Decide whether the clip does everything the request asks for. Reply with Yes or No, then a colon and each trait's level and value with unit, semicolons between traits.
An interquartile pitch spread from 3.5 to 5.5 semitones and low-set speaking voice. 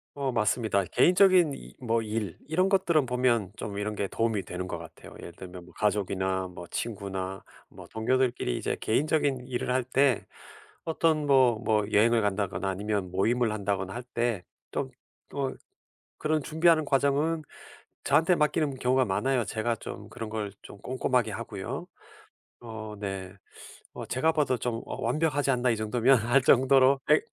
Yes: average, 5.1 semitones; low, 120 Hz